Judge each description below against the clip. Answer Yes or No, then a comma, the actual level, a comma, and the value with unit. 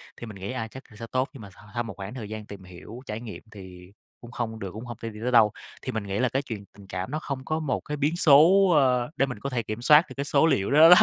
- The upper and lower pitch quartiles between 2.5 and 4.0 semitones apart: No, average, 4.7 semitones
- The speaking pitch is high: No, low, 120 Hz